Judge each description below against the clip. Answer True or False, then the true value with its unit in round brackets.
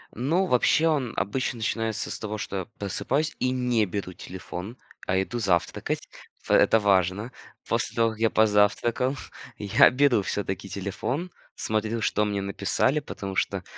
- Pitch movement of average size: True (4.0 semitones)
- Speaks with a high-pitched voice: False (110 Hz)